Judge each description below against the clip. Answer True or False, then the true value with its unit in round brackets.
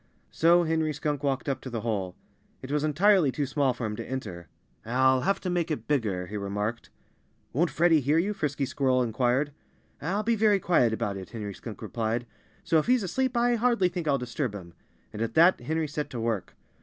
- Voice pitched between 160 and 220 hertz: False (140 Hz)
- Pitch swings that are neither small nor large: False (6.5 semitones)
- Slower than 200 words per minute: False (205 wpm)